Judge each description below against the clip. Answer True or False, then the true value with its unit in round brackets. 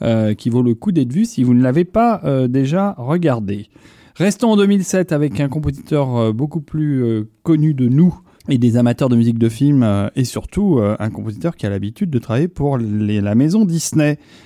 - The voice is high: False (135 Hz)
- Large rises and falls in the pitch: True (6.1 semitones)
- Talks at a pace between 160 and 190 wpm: False (210 wpm)